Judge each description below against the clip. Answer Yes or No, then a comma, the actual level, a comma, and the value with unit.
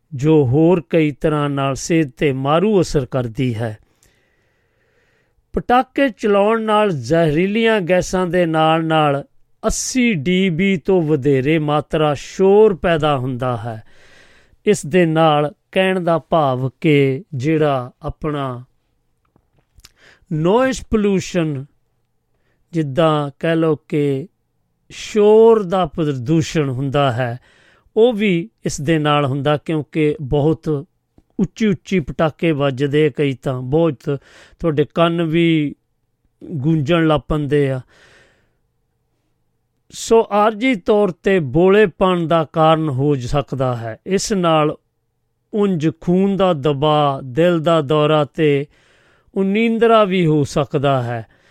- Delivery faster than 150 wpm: No, average, 110 wpm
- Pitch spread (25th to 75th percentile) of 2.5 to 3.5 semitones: No, average, 4.5 semitones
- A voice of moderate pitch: Yes, medium, 155 Hz